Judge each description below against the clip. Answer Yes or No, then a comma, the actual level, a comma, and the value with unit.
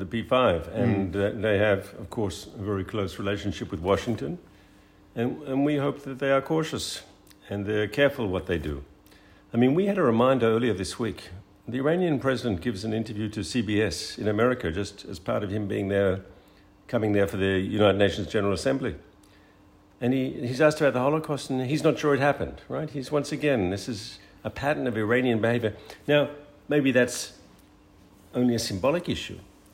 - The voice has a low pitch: Yes, low, 110 Hz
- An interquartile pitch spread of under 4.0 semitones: No, average, 4.9 semitones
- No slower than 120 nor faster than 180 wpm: No, average, 190 wpm